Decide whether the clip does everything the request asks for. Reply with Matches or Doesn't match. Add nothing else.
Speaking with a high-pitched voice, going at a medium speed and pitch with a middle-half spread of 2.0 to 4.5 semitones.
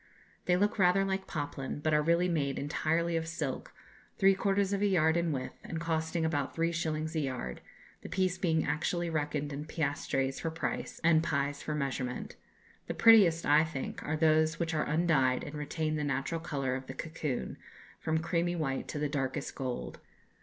Doesn't match